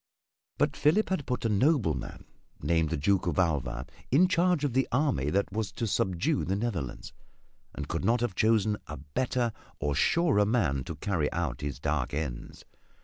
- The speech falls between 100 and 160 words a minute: No, average, 175 wpm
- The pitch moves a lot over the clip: Yes, wide, 8.6 semitones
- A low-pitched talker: Yes, very low, 95 Hz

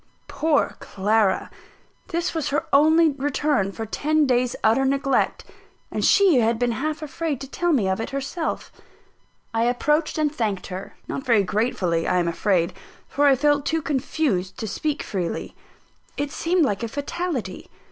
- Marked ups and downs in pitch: Yes, wide, 5.9 semitones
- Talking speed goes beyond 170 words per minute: No, average, 160 wpm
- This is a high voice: Yes, very high, 270 Hz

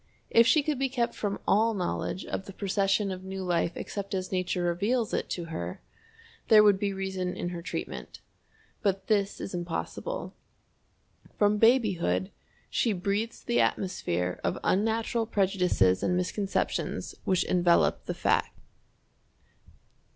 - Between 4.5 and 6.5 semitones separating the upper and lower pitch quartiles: No, average, 3.1 semitones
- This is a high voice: Yes, high, 195 Hz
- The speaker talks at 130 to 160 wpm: Yes, average, 140 wpm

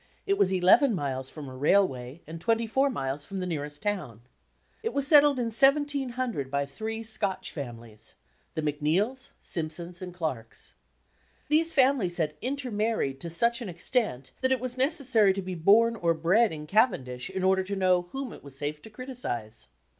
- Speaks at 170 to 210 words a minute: Yes, average, 180 wpm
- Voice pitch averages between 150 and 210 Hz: Yes, high, 190 Hz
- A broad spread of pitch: Yes, wide, 8.4 semitones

